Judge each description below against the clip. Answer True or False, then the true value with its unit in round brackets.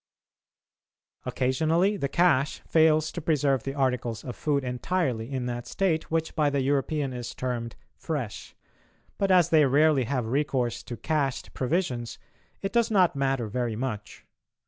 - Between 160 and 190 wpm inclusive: False (145 wpm)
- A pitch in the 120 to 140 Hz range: True (135 Hz)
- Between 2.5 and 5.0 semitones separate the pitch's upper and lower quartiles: True (4.2 semitones)